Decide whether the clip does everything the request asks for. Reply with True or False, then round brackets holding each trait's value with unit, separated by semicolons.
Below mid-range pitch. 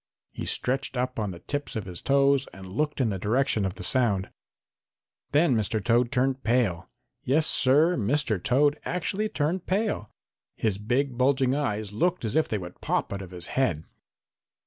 True (125 Hz)